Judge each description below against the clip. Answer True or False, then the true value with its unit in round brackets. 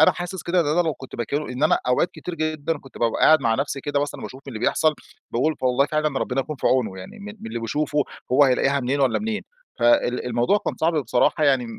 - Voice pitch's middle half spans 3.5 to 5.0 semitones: True (3.8 semitones)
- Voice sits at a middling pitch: True (145 Hz)